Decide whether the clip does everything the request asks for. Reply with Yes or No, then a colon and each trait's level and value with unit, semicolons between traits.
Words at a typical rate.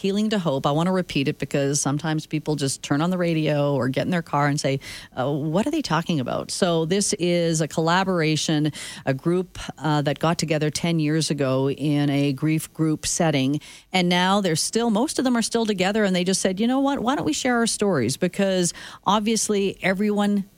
No: fast, 215 wpm